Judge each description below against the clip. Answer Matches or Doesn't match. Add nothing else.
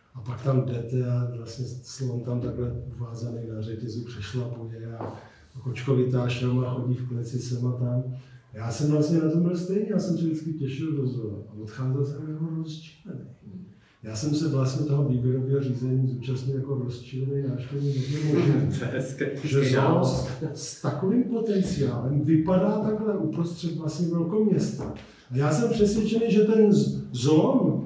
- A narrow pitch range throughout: Doesn't match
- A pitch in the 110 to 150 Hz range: Matches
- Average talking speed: Matches